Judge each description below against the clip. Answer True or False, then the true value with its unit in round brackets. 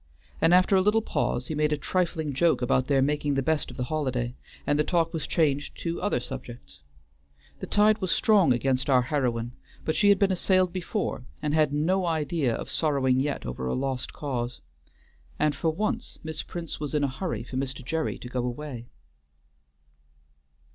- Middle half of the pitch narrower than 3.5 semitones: False (4.7 semitones)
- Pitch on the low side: False (150 Hz)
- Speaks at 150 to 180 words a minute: False (190 wpm)